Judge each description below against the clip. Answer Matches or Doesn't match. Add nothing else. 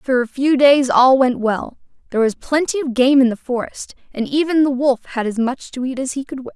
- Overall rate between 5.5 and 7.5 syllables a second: Doesn't match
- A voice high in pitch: Matches